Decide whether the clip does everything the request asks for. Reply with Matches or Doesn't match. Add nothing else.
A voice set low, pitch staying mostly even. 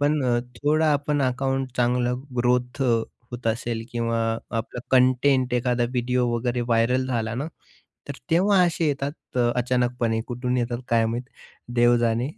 Matches